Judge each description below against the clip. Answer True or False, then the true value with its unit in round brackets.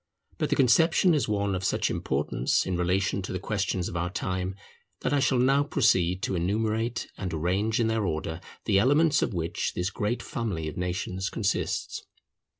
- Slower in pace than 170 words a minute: False (180 wpm)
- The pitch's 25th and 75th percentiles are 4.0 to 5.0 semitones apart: True (4.3 semitones)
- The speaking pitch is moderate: False (100 Hz)